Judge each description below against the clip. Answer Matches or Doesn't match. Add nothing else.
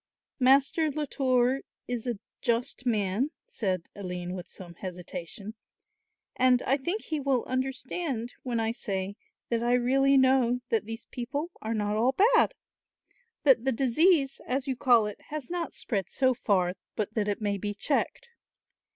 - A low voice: Doesn't match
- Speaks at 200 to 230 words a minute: Doesn't match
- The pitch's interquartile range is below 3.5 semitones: Doesn't match